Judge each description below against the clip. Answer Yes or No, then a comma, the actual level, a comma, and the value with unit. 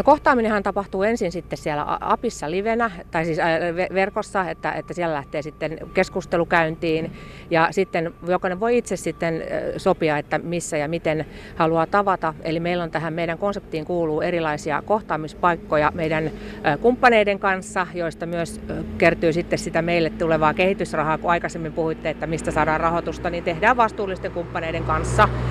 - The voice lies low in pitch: No, medium, 170 Hz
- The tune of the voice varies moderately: Yes, average, 3.0 semitones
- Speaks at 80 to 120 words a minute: No, average, 145 wpm